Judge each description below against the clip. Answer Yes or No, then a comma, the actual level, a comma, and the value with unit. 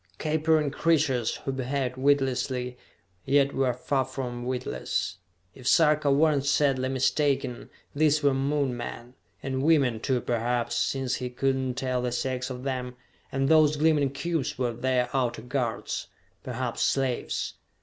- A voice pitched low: Yes, low, 130 Hz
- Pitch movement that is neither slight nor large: No, narrow, 2.2 semitones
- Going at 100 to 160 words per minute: Yes, average, 145 wpm